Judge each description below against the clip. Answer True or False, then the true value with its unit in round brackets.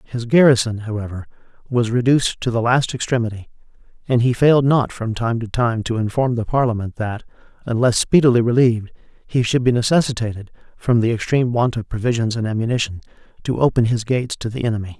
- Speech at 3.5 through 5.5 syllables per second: False (6.2 syllables/s)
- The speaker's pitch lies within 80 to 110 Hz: False (120 Hz)